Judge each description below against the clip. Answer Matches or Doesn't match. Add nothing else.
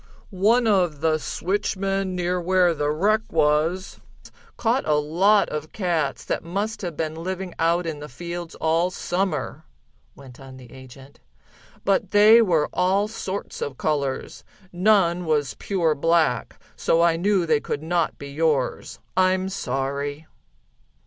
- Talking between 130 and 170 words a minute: Matches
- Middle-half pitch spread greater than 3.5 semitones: Matches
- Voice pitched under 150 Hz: Doesn't match